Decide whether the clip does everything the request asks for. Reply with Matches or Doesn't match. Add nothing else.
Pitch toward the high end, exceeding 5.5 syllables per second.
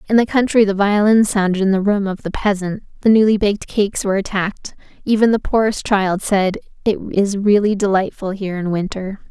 Matches